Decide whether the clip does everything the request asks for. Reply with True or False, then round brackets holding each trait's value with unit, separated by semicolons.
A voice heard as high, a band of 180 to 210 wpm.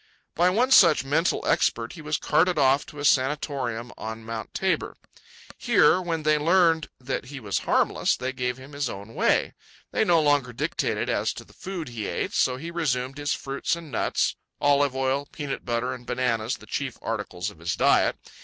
False (135 Hz; 185 wpm)